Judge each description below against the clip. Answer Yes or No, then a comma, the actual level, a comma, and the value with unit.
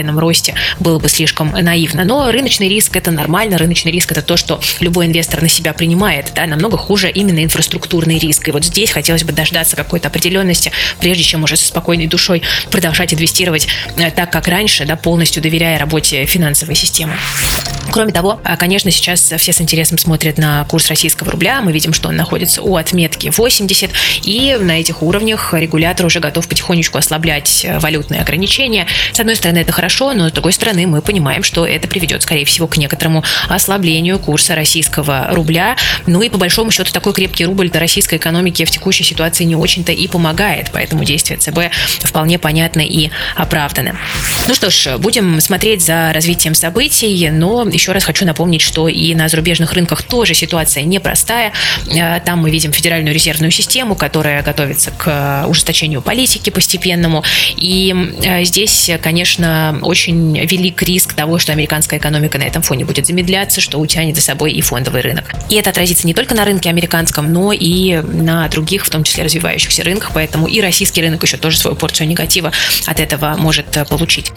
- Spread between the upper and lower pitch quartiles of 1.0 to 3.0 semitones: Yes, narrow, 2.4 semitones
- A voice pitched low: No, medium, 165 Hz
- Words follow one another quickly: Yes, fast, 175 wpm